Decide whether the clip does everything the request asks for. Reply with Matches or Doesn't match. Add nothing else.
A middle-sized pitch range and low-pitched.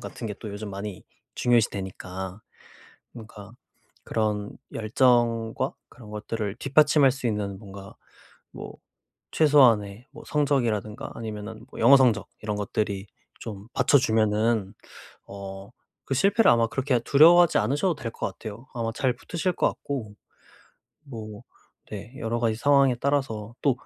Matches